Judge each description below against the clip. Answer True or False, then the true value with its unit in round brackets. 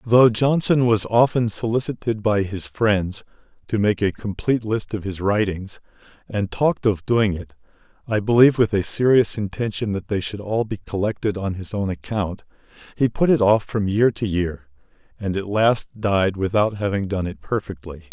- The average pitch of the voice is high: False (105 Hz)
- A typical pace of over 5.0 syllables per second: False (4.9 syllables/s)